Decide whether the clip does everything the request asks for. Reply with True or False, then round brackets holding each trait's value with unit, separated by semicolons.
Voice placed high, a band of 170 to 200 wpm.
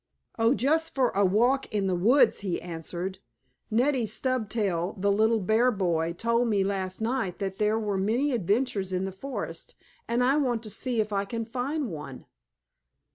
True (215 Hz; 175 wpm)